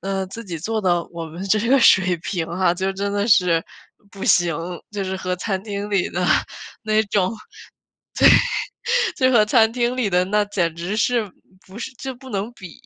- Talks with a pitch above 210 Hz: No, high, 195 Hz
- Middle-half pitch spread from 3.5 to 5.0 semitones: No, average, 3.1 semitones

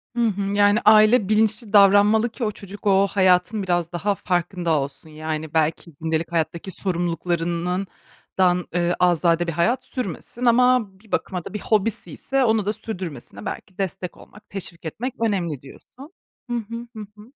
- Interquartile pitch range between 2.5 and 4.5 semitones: Yes, average, 4.0 semitones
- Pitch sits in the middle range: No, high, 195 Hz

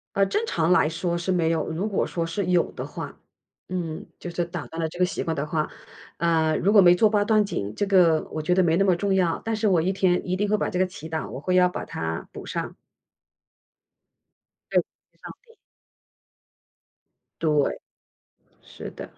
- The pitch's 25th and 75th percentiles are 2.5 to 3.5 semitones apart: Yes, average, 2.9 semitones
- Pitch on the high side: No, medium, 175 Hz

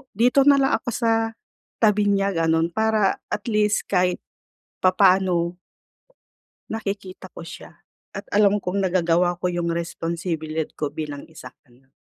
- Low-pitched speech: No, medium, 185 Hz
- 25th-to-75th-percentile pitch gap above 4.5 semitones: No, average, 3.7 semitones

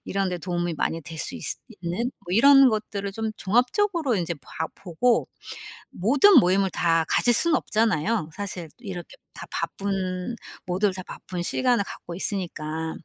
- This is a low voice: No, high, 195 Hz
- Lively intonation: No, average, 4.9 semitones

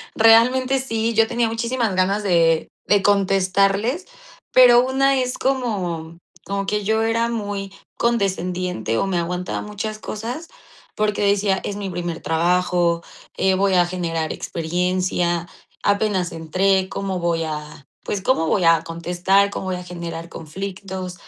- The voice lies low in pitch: No, high, 195 Hz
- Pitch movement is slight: No, average, 3.7 semitones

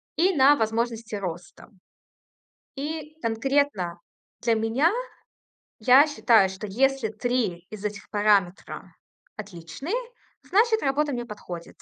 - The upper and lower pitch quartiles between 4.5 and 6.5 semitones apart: Yes, wide, 5.6 semitones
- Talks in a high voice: Yes, high, 230 Hz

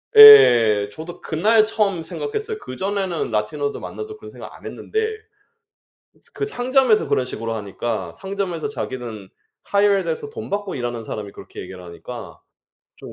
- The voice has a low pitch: No, high, 190 Hz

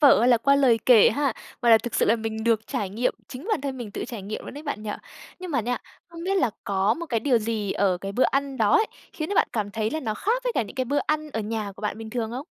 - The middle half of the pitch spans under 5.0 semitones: Yes, average, 4.5 semitones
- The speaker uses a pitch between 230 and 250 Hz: Yes, high, 235 Hz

